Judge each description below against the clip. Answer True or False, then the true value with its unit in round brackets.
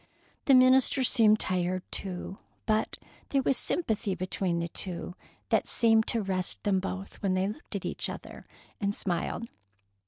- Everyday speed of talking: True (155 wpm)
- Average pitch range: True (3.7 semitones)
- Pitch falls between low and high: False (200 Hz)